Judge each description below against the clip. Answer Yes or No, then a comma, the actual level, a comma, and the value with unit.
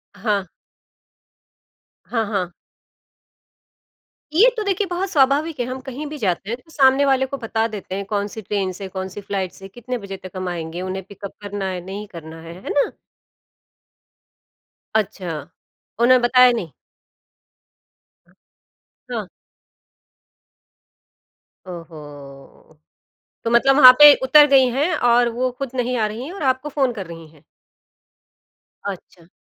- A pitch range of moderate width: No, wide, 6.0 semitones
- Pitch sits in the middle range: No, high, 220 Hz